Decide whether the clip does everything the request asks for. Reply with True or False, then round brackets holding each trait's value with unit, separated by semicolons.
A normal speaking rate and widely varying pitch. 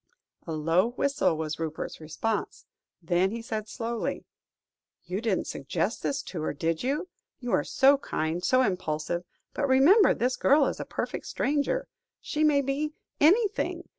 True (155 wpm; 9.0 semitones)